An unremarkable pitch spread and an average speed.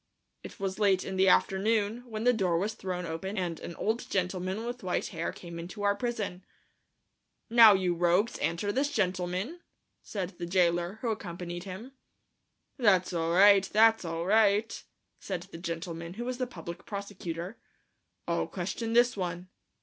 Yes: average, 3.8 semitones; average, 160 wpm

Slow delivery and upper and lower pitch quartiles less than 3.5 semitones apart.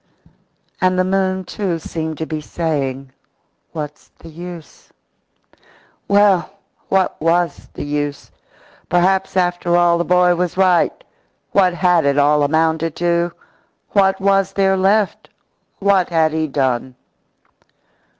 Yes: slow, 120 wpm; average, 3.1 semitones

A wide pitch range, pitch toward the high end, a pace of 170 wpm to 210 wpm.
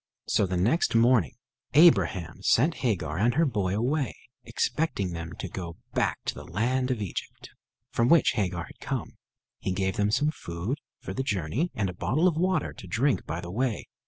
No: wide, 6.5 semitones; low, 110 Hz; average, 190 wpm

